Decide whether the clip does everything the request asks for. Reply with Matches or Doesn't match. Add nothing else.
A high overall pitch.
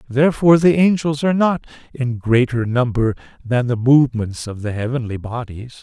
Doesn't match